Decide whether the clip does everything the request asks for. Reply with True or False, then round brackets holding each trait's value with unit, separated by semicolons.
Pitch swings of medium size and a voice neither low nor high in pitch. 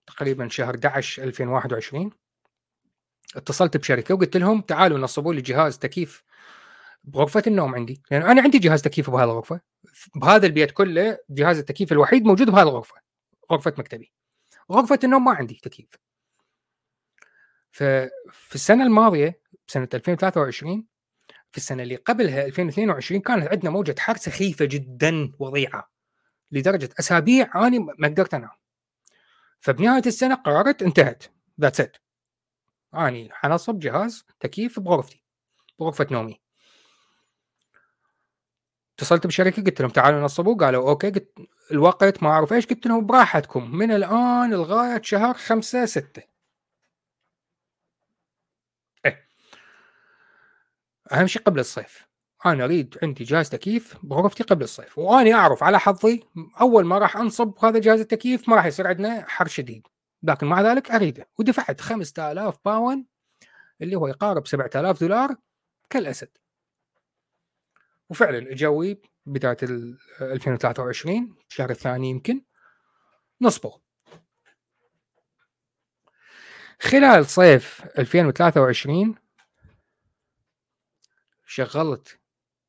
False (7.6 semitones; 175 Hz)